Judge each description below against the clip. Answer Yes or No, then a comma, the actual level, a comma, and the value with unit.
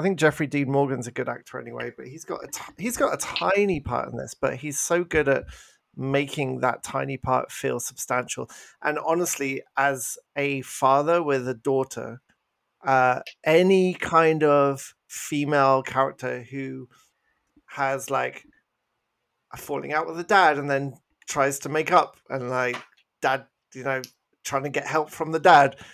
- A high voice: No, medium, 140 Hz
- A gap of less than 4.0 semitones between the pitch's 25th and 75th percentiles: Yes, narrow, 2.6 semitones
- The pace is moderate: Yes, average, 170 wpm